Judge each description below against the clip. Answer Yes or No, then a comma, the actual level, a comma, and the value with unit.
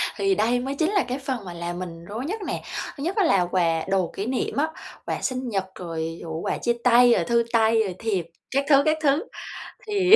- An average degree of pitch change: No, wide, 7.2 semitones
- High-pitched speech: Yes, high, 235 Hz